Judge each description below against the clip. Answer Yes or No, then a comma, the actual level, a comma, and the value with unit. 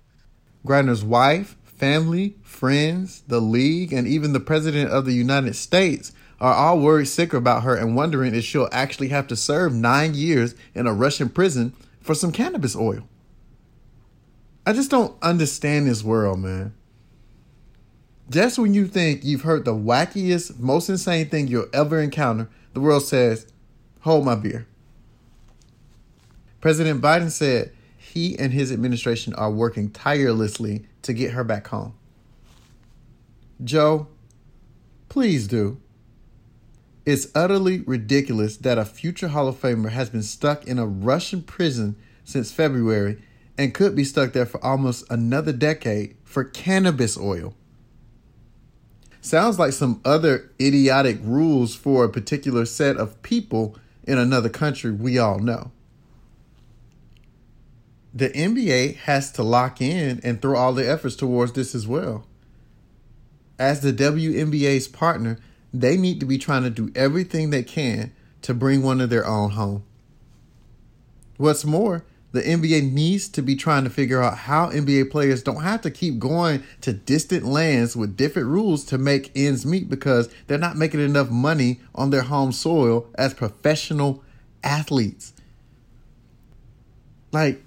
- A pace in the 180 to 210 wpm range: No, average, 145 wpm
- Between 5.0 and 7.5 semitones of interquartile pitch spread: No, average, 3.9 semitones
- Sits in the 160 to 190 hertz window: No, low, 130 Hz